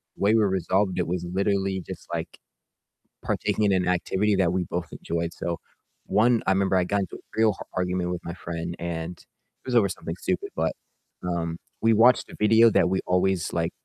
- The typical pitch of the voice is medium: No, very low, 95 Hz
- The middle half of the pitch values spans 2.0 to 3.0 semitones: Yes, average, 2.7 semitones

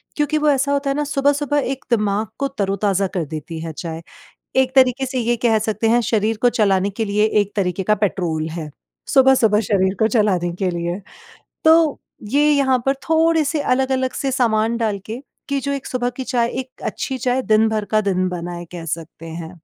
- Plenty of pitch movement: Yes, wide, 5.8 semitones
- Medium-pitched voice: No, high, 225 Hz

